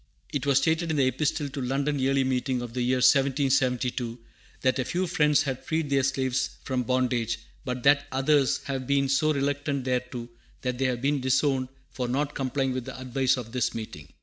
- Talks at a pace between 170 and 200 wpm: Yes, average, 195 wpm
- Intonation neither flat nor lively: No, narrow, 1.9 semitones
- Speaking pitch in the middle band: No, low, 130 Hz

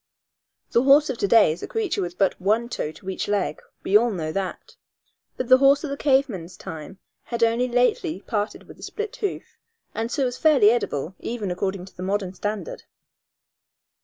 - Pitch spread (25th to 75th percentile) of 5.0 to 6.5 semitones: Yes, wide, 5.4 semitones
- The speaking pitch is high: Yes, high, 215 Hz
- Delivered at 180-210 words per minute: Yes, average, 195 wpm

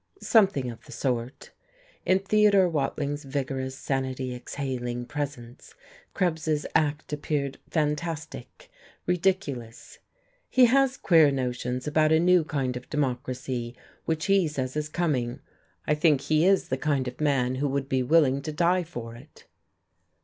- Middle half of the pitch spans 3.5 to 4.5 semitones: Yes, average, 3.8 semitones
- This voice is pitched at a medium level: Yes, medium, 145 Hz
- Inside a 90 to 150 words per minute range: Yes, average, 140 wpm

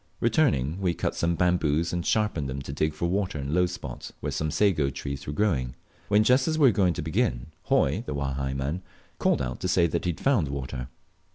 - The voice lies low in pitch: Yes, very low, 80 Hz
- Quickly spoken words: Yes, fast, 220 wpm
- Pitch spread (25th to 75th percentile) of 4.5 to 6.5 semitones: Yes, average, 5.2 semitones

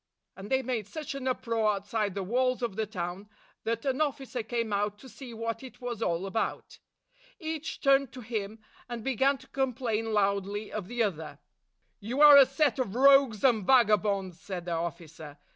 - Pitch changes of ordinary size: Yes, average, 4.6 semitones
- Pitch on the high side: Yes, high, 225 Hz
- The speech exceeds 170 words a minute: Yes, average, 185 wpm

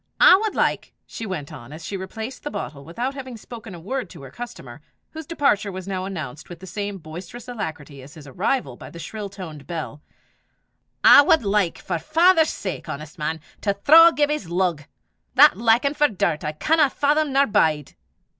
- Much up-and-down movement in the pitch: Yes, wide, 8.7 semitones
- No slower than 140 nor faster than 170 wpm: No, average, 190 wpm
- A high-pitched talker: Yes, high, 195 Hz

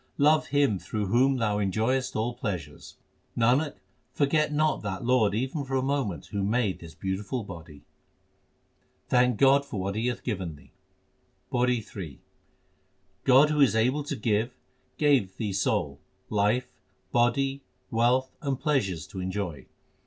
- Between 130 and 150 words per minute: Yes, average, 145 wpm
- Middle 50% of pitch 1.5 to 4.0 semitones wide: No, average, 5.2 semitones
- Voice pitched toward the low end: Yes, low, 120 Hz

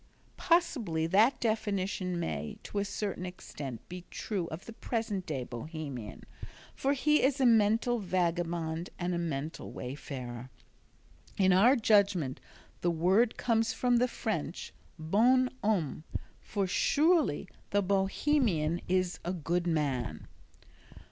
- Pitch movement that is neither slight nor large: No, wide, 5.8 semitones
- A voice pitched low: No, medium, 185 Hz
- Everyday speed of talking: No, slow, 125 wpm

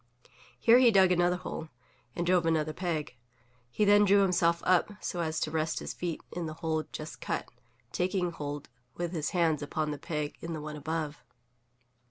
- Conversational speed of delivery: Yes, average, 185 wpm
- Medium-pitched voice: Yes, medium, 165 Hz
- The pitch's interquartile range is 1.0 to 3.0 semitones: Yes, narrow, 2.6 semitones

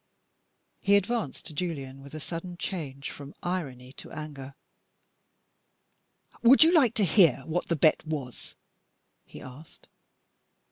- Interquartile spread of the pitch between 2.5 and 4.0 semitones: No, average, 5.2 semitones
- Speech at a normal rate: No, slow, 130 wpm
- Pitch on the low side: No, medium, 155 Hz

